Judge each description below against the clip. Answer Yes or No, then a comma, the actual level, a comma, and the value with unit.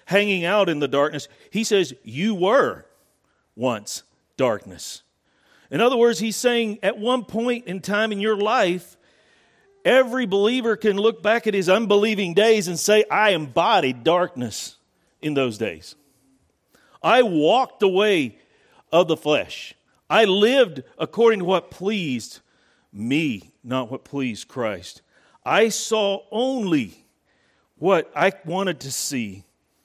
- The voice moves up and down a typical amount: No, wide, 6.4 semitones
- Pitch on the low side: No, high, 195 Hz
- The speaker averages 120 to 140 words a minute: Yes, slow, 135 wpm